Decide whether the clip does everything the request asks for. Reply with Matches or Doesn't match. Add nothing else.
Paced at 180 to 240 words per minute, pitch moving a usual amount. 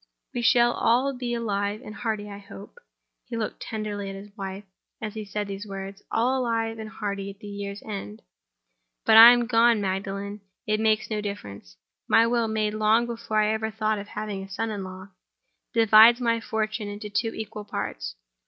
Doesn't match